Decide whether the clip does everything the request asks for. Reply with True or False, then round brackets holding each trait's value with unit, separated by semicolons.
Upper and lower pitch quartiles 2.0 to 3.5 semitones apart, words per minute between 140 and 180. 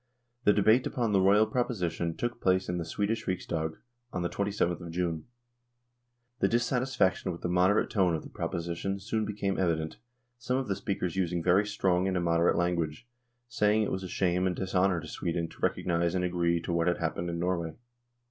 False (3.1 semitones; 195 wpm)